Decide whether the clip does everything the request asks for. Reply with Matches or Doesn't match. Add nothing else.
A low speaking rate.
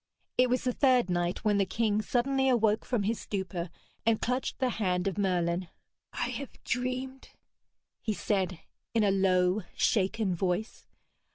Doesn't match